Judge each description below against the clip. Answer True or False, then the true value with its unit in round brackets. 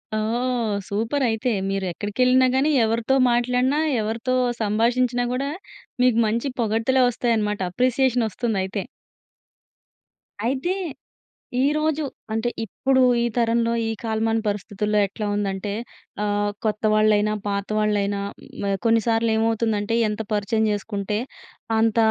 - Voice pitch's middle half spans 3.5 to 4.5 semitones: False (2.8 semitones)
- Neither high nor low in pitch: False (225 Hz)